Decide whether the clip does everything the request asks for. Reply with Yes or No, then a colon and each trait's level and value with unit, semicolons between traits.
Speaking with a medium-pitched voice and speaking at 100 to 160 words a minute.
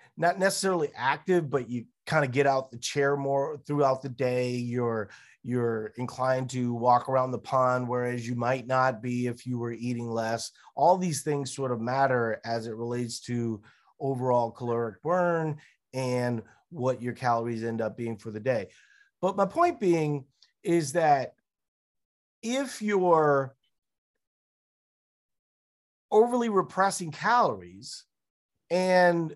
No: low, 130 Hz; average, 140 wpm